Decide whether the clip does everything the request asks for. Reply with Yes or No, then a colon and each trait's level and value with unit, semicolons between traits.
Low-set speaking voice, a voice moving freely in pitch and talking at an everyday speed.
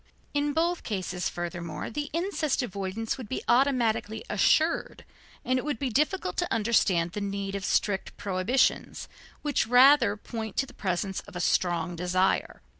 No: high, 220 Hz; wide, 6.4 semitones; average, 155 wpm